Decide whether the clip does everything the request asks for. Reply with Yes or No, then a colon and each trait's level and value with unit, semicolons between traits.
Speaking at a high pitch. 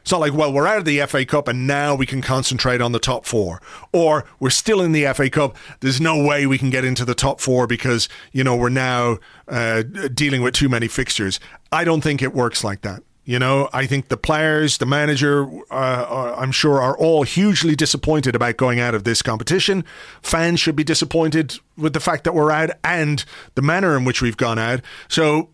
No: medium, 140 Hz